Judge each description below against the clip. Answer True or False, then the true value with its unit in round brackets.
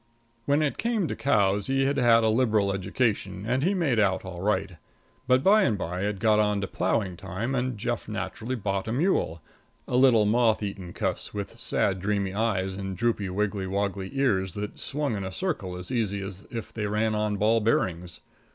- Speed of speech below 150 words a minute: False (195 wpm)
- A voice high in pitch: False (105 Hz)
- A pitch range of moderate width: True (3.9 semitones)